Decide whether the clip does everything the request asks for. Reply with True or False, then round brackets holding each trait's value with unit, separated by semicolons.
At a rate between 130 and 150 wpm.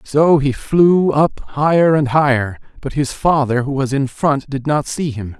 False (200 wpm)